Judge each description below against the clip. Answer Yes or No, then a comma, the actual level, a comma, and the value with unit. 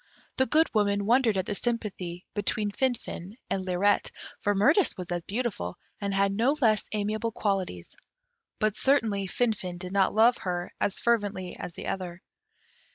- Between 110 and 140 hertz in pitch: No, high, 205 Hz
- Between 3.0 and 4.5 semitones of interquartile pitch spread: Yes, average, 3.4 semitones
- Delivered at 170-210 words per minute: No, average, 160 wpm